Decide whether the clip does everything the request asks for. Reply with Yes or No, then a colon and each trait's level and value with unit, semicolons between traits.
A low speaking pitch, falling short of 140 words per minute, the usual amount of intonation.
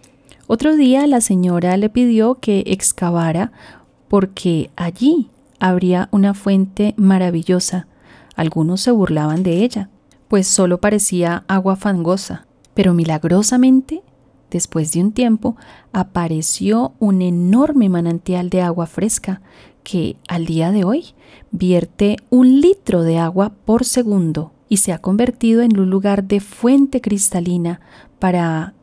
No: high, 195 Hz; slow, 125 wpm; average, 4.3 semitones